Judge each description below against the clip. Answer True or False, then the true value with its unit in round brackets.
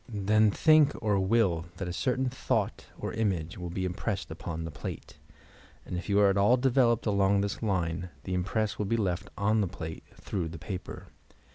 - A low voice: True (100 Hz)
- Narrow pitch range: False (3.6 semitones)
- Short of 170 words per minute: False (190 wpm)